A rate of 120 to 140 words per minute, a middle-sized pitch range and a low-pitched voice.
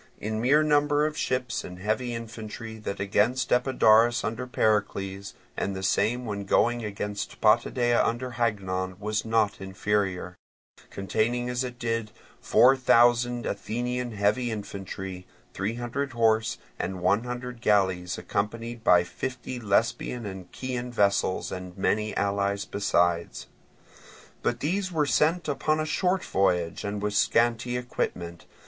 Yes: slow, 135 wpm; average, 3.6 semitones; low, 110 Hz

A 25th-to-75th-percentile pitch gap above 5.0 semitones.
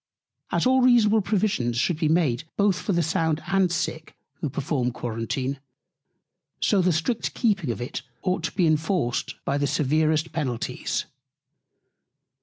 Yes: wide, 5.4 semitones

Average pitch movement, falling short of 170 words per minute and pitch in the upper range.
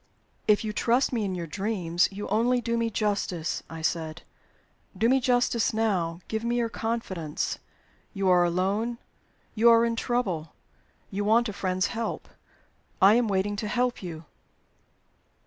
Yes: average, 4.1 semitones; average, 155 wpm; high, 210 Hz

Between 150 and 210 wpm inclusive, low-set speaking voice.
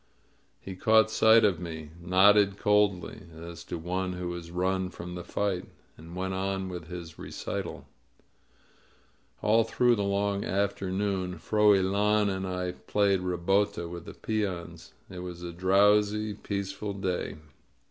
No: slow, 135 wpm; very low, 95 Hz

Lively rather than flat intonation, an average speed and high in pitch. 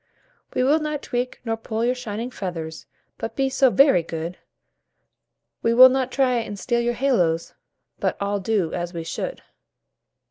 Yes: wide, 5.9 semitones; average, 170 wpm; high, 230 Hz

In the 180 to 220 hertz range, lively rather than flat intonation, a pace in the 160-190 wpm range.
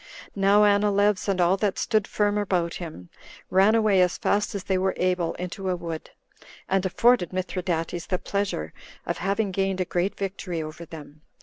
No: high, 190 Hz; narrow, 2.5 semitones; average, 175 wpm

